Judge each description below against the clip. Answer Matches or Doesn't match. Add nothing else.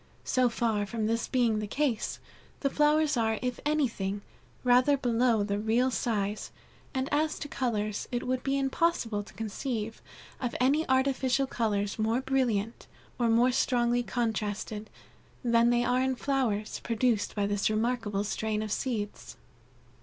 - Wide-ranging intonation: Doesn't match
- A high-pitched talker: Matches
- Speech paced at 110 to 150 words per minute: Matches